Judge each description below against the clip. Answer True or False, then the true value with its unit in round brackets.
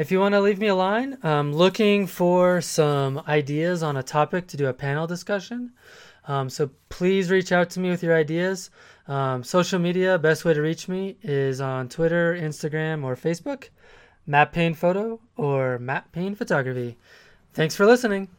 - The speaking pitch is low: False (170 Hz)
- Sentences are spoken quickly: False (180 wpm)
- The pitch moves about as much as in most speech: True (4.2 semitones)